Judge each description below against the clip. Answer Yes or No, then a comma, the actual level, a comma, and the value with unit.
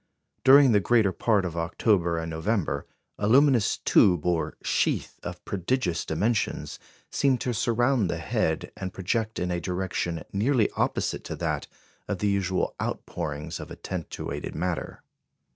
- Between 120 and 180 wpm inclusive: Yes, average, 145 wpm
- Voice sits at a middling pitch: No, very low, 95 Hz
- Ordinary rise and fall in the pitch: Yes, average, 5.0 semitones